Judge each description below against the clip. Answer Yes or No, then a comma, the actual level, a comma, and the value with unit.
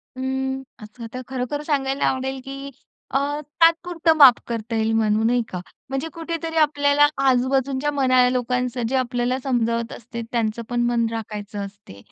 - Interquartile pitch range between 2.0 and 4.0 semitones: Yes, average, 2.8 semitones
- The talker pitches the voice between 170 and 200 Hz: No, very high, 255 Hz